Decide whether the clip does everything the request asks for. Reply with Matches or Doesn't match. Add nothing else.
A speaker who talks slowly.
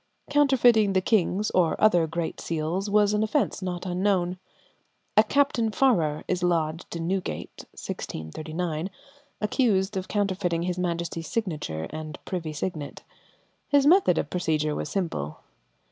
Matches